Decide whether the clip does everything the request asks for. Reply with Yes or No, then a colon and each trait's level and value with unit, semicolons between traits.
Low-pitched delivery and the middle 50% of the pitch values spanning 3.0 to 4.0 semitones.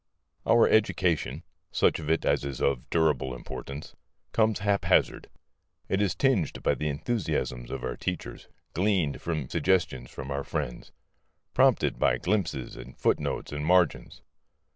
No: very low, 80 Hz; wide, 5.5 semitones